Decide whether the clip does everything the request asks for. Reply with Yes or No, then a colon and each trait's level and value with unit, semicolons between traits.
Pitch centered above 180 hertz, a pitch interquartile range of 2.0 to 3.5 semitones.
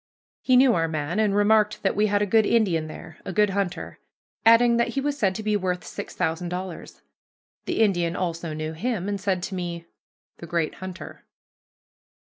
No: high, 190 Hz; average, 3.9 semitones